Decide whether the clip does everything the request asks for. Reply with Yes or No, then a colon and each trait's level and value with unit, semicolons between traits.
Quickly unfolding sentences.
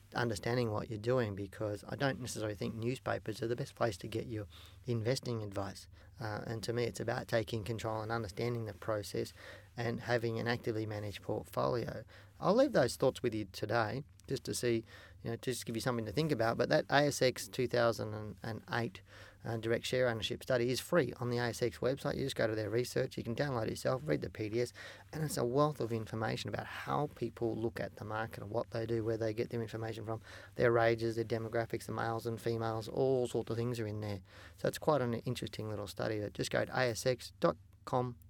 Yes: fast, 210 wpm